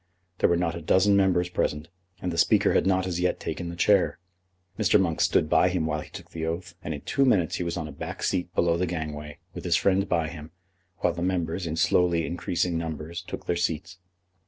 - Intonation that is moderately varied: No, narrow, 1.9 semitones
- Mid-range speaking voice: No, very low, 85 Hz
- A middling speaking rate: No, fast, 230 wpm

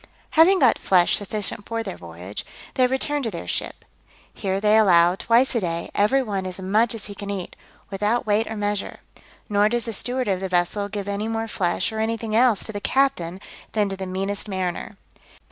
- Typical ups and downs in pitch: Yes, average, 3.0 semitones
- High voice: Yes, high, 205 Hz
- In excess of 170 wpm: Yes, average, 200 wpm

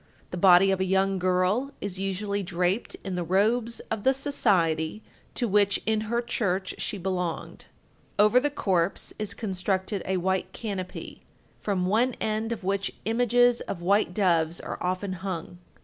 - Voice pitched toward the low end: No, high, 195 Hz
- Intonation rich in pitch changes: No, average, 2.9 semitones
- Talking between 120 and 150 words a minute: No, average, 160 wpm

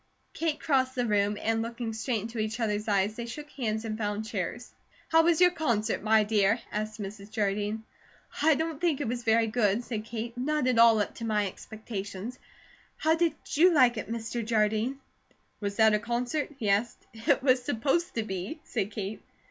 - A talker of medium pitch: No, high, 225 Hz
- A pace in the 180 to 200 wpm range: Yes, average, 190 wpm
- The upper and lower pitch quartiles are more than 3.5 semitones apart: No, average, 3.2 semitones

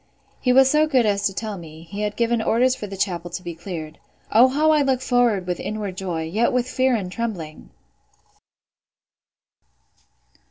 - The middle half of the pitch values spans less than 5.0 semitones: No, wide, 5.6 semitones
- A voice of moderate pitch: No, high, 210 Hz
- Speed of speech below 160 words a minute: No, average, 175 wpm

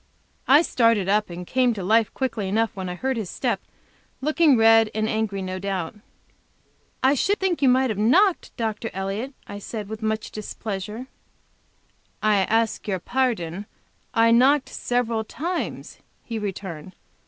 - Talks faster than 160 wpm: No, average, 155 wpm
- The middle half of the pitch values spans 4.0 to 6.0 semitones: Yes, average, 4.3 semitones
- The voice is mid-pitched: No, high, 220 Hz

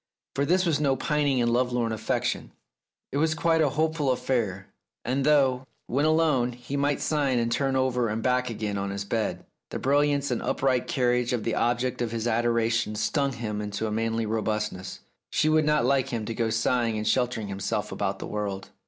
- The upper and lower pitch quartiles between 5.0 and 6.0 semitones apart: No, average, 3.8 semitones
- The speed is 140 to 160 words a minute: No, average, 195 wpm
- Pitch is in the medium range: No, low, 125 Hz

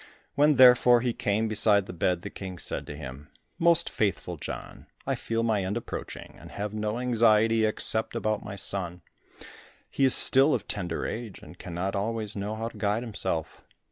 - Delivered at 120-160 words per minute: No, average, 180 wpm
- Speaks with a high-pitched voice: No, low, 110 Hz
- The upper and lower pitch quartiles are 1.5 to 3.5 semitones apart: Yes, average, 3.1 semitones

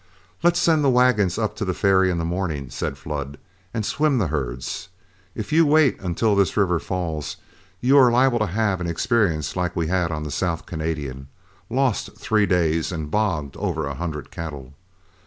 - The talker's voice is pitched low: Yes, very low, 90 Hz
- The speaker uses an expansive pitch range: Yes, wide, 6.1 semitones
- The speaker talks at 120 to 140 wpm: No, average, 185 wpm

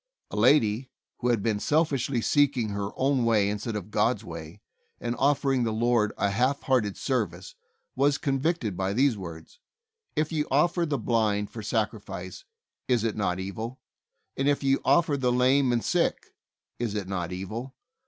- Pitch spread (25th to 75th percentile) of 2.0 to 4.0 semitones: No, average, 4.8 semitones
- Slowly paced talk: No, average, 170 wpm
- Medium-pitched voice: No, low, 120 Hz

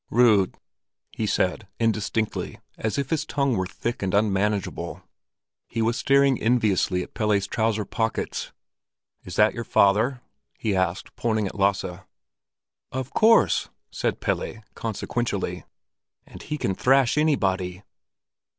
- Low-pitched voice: Yes, low, 110 Hz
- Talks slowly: Yes, slow, 125 wpm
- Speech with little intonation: No, average, 3.8 semitones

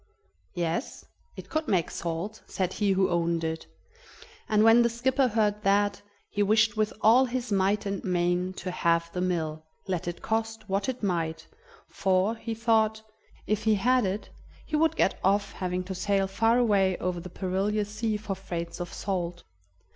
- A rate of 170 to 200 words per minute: Yes, average, 175 wpm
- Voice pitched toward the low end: No, high, 200 Hz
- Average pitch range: Yes, average, 3.4 semitones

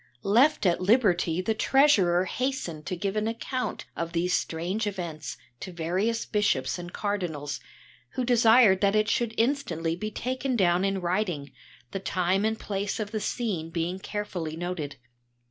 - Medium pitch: No, high, 195 Hz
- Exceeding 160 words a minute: No, average, 155 wpm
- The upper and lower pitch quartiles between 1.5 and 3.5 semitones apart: No, average, 4.2 semitones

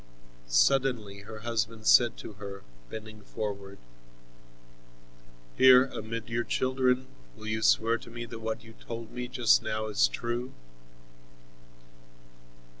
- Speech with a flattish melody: Yes, narrow, 2.1 semitones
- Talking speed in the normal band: No, slow, 120 wpm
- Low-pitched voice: Yes, low, 110 Hz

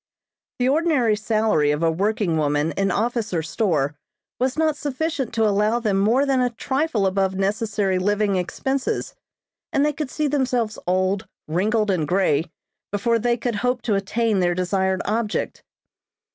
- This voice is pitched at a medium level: No, high, 210 Hz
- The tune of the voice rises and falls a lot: No, average, 4.7 semitones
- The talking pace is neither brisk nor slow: Yes, average, 160 wpm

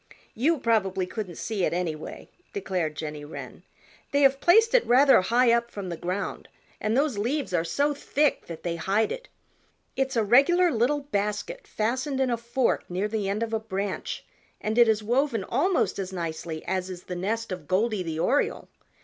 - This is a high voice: Yes, high, 220 Hz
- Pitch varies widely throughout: Yes, wide, 6.3 semitones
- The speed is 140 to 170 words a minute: No, average, 185 wpm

